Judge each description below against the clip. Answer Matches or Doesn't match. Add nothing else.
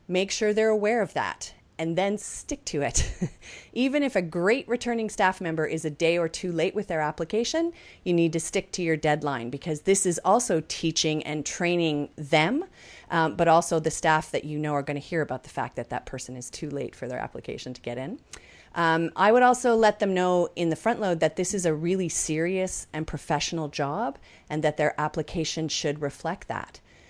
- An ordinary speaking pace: Doesn't match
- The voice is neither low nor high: Matches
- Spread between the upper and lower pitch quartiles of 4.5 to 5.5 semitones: Doesn't match